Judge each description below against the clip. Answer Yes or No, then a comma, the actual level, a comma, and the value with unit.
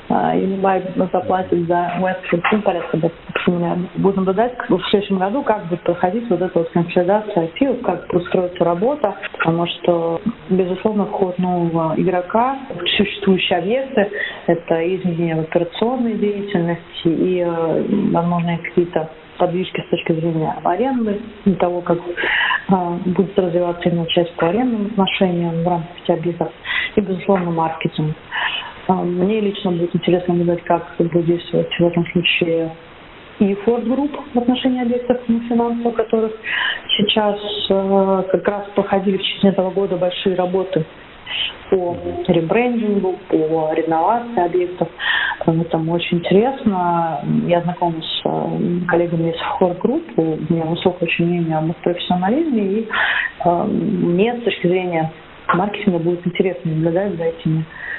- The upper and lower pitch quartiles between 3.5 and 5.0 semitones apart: No, average, 2.9 semitones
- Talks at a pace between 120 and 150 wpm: Yes, average, 135 wpm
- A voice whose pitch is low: No, medium, 180 Hz